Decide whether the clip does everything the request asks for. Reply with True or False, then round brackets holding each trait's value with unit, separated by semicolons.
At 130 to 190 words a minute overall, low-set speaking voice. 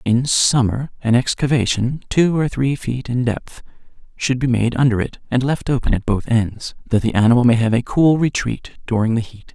False (200 wpm; 125 Hz)